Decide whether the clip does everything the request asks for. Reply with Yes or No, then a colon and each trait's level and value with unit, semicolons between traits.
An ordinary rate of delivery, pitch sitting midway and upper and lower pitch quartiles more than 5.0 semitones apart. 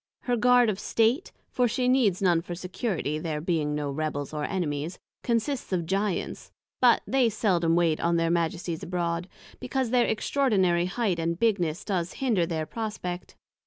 Yes: average, 165 wpm; medium, 180 Hz; wide, 5.5 semitones